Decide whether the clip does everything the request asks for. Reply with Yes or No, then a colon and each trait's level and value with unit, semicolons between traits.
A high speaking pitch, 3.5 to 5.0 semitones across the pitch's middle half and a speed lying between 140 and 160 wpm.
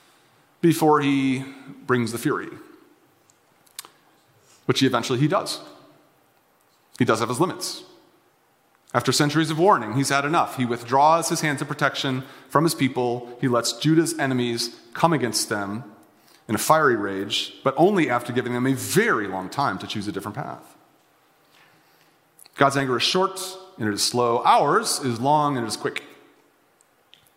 No: low, 135 Hz; average, 3.8 semitones; average, 150 wpm